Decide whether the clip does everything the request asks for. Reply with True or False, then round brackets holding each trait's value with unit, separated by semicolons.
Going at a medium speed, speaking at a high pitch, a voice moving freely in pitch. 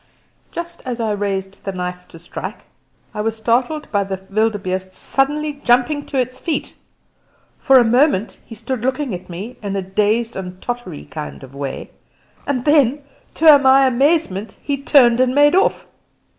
True (165 wpm; 235 Hz; 5.9 semitones)